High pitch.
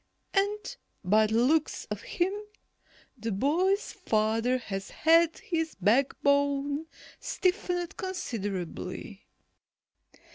Yes: very high, 280 Hz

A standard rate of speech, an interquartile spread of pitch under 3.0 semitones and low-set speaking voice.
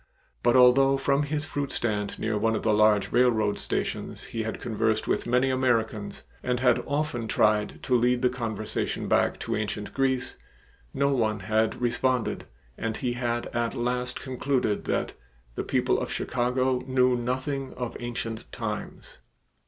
Yes: average, 155 wpm; narrow, 2.6 semitones; low, 120 Hz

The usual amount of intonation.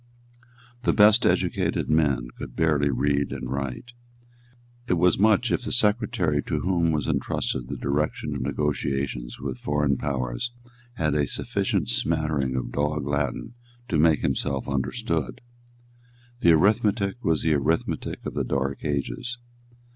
Yes: average, 3.6 semitones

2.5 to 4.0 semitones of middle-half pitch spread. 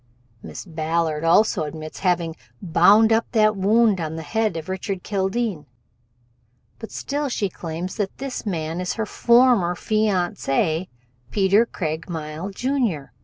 No: average, 5.0 semitones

